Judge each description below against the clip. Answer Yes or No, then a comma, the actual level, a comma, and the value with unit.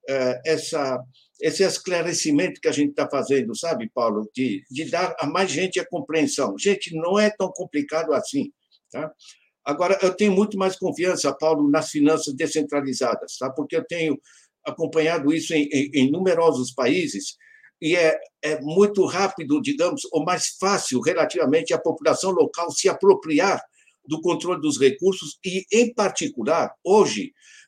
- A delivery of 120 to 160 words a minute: Yes, average, 150 wpm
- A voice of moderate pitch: Yes, medium, 170 Hz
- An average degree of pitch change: Yes, average, 4.8 semitones